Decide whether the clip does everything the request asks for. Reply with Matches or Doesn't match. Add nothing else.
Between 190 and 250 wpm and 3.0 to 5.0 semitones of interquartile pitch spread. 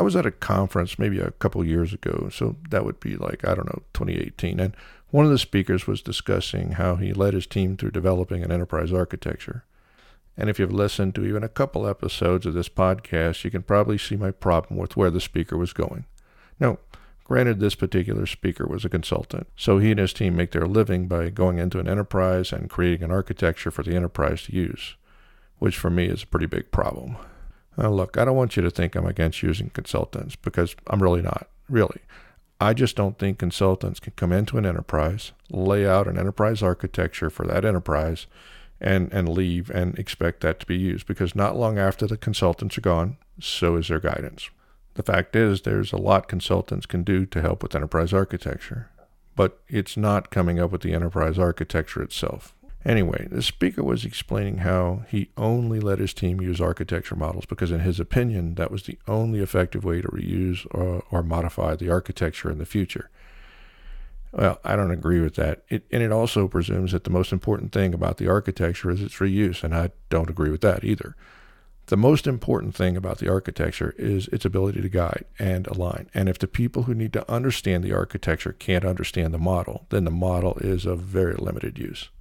Doesn't match